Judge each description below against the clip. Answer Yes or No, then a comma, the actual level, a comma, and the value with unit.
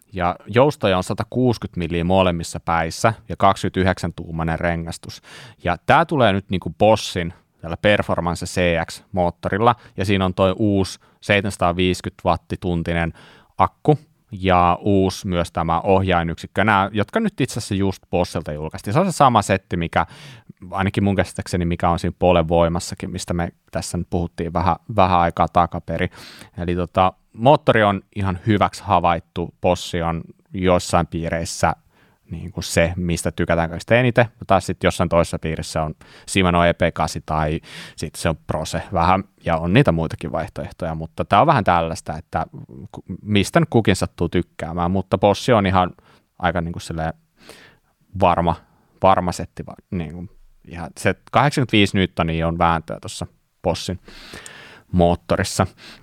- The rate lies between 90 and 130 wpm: No, average, 140 wpm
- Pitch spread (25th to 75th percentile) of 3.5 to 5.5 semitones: No, average, 2.8 semitones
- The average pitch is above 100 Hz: No, very low, 90 Hz